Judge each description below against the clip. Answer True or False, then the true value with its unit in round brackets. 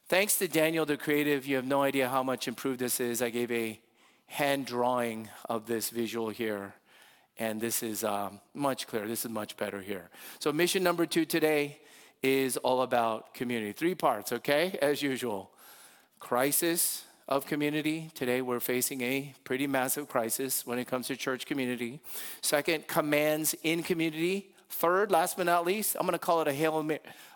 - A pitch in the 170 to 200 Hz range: False (135 Hz)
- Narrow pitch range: False (4.7 semitones)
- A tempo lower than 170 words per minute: False (175 wpm)